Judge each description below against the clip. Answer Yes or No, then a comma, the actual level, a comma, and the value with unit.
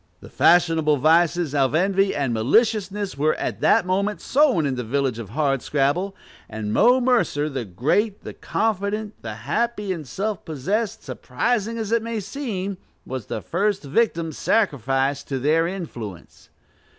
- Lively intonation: Yes, wide, 7.2 semitones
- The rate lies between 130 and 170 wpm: Yes, average, 145 wpm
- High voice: No, medium, 170 Hz